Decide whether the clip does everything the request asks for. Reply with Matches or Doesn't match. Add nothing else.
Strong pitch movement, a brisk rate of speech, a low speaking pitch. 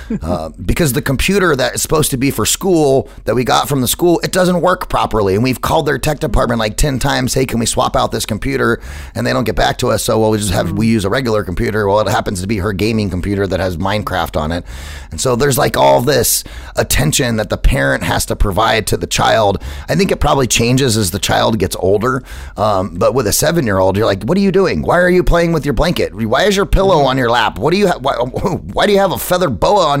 Matches